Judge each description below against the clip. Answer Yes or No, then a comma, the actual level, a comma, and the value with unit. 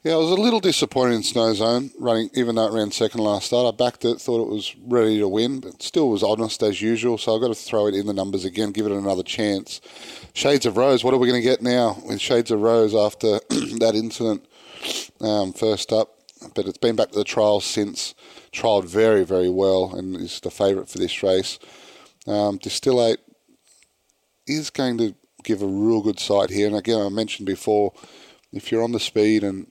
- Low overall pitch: Yes, low, 110 Hz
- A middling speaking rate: No, fast, 215 wpm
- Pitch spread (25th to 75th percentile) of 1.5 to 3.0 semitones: Yes, narrow, 2.5 semitones